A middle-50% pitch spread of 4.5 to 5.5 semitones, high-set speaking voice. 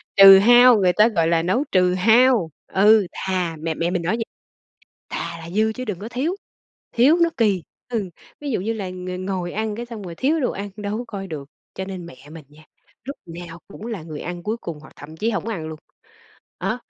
Yes: average, 4.8 semitones; high, 195 Hz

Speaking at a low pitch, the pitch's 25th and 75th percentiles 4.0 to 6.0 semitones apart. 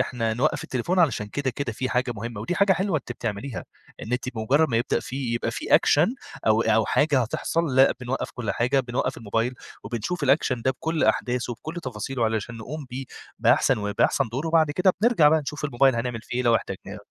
Yes: low, 125 Hz; average, 4.3 semitones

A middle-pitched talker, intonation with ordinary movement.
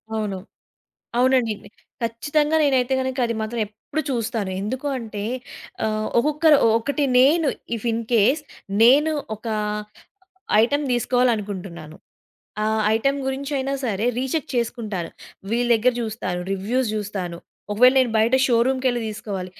No: high, 235 Hz; average, 3.8 semitones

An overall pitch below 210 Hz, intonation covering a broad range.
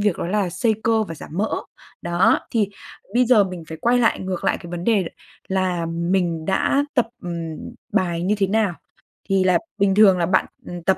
No: medium, 185 Hz; average, 3.4 semitones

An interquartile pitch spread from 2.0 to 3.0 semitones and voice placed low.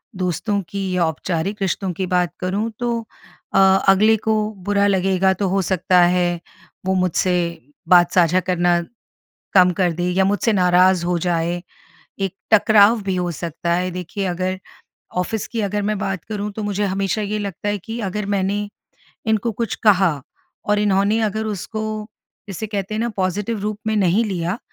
No: narrow, 2.4 semitones; high, 195 Hz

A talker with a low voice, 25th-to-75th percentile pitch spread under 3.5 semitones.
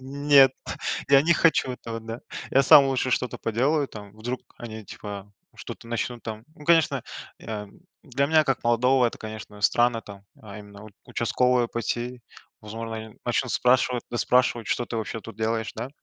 Yes: low, 120 Hz; average, 2.9 semitones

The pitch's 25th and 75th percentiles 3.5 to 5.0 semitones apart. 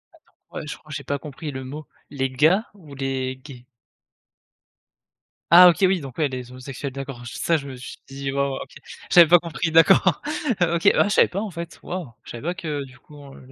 Yes: average, 4.1 semitones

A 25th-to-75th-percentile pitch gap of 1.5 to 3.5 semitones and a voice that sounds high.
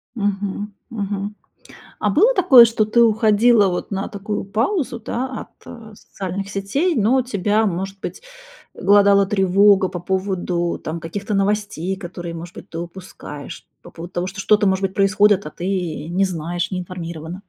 Yes: average, 2.7 semitones; high, 195 Hz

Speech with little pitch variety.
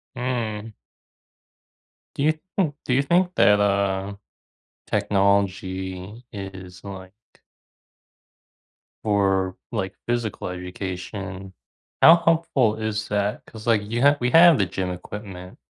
No: average, 4.0 semitones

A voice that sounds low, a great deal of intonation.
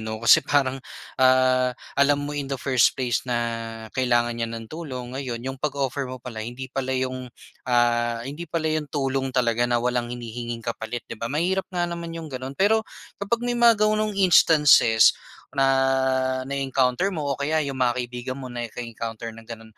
No: low, 130 Hz; average, 3.4 semitones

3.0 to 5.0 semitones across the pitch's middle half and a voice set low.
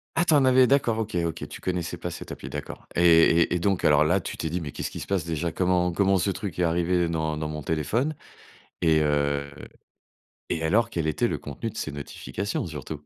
Yes: average, 3.7 semitones; very low, 85 Hz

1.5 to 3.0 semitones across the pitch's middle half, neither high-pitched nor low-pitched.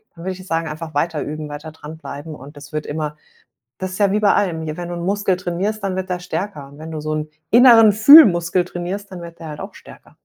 No: average, 3.7 semitones; medium, 170 Hz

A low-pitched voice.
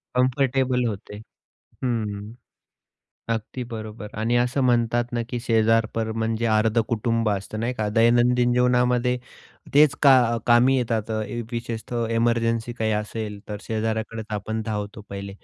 Yes: low, 115 Hz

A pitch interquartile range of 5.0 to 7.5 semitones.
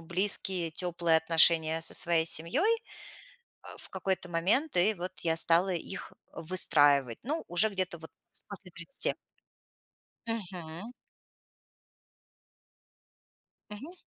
No: average, 3.1 semitones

